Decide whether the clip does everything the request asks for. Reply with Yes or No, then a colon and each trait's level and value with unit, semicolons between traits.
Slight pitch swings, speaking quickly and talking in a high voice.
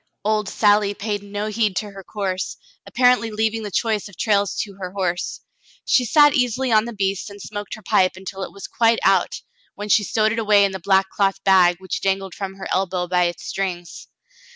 Yes: narrow, 2.2 semitones; fast, 210 wpm; high, 200 Hz